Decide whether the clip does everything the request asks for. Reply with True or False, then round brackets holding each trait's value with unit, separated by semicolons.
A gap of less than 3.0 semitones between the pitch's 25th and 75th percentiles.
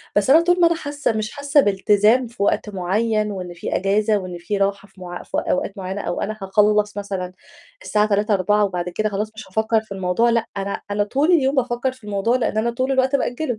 False (3.6 semitones)